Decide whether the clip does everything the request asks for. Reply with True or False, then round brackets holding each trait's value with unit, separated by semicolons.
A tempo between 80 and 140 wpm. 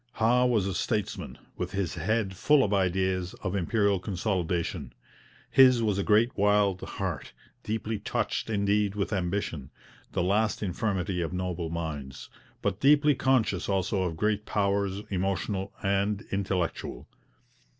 True (135 wpm)